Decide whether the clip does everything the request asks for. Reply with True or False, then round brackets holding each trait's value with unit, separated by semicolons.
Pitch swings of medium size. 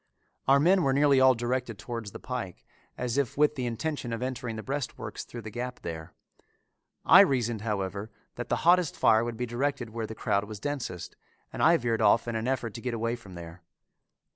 True (3.2 semitones)